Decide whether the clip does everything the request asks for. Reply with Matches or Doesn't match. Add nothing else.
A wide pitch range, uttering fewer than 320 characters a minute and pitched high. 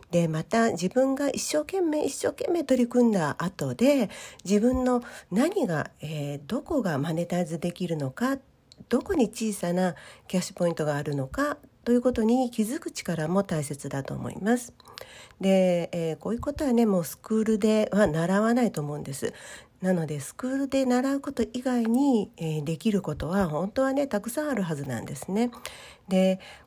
Doesn't match